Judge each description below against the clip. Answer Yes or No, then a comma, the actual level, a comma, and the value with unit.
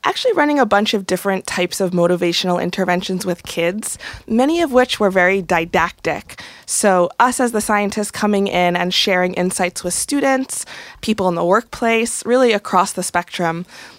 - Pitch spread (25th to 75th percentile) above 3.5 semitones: Yes, average, 4.2 semitones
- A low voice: No, high, 190 Hz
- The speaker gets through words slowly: No, average, 165 wpm